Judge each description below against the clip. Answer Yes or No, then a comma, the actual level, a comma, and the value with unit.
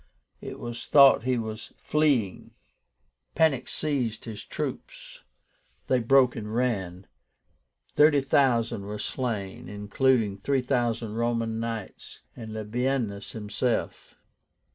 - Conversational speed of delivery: No, slow, 105 wpm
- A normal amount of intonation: Yes, average, 3.4 semitones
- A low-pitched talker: Yes, low, 115 Hz